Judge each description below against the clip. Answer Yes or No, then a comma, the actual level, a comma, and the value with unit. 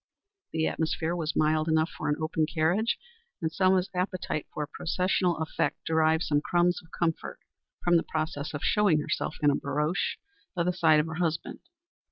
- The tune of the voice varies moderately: No, narrow, 2.1 semitones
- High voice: No, medium, 160 Hz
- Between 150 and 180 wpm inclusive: Yes, average, 175 wpm